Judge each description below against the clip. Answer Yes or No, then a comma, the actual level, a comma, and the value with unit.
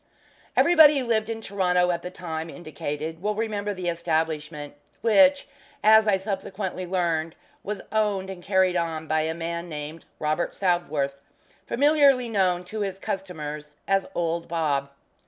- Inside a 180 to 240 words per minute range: No, average, 145 wpm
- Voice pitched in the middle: Yes, medium, 180 Hz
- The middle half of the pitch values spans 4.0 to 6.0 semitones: Yes, average, 4.3 semitones